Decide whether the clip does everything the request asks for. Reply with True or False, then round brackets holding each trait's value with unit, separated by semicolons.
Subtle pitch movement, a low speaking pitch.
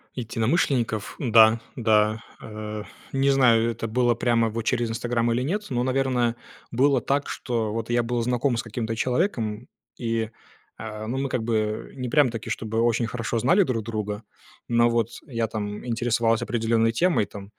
True (1.8 semitones; 115 Hz)